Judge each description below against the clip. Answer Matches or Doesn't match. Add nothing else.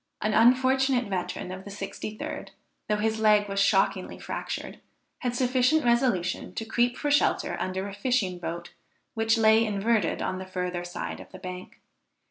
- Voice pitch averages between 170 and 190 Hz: Doesn't match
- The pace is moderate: Matches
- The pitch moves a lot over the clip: Doesn't match